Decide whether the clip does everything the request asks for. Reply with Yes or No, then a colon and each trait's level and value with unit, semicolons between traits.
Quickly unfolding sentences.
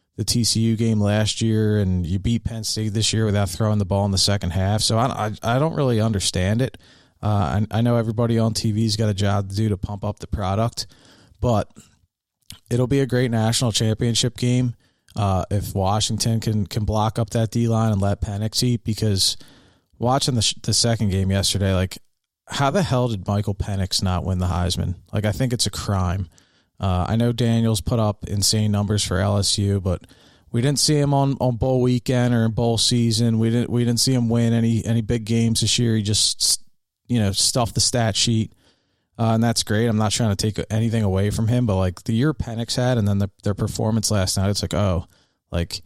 Yes: fast, 220 wpm